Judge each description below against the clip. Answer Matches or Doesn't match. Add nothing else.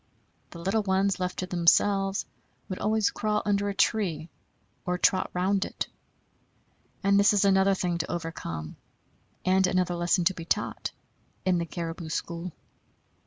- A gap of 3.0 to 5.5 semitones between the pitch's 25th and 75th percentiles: Doesn't match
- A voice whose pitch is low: Doesn't match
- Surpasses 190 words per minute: Doesn't match